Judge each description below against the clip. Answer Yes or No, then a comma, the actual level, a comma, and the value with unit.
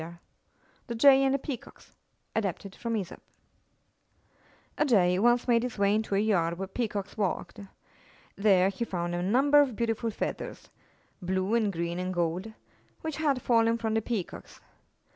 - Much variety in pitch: No, average, 4.1 semitones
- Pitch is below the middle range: No, high, 215 Hz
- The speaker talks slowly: No, average, 150 wpm